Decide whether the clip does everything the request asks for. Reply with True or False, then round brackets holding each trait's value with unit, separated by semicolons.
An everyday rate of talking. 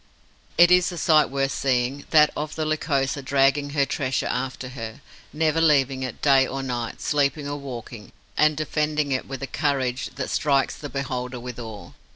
True (180 wpm)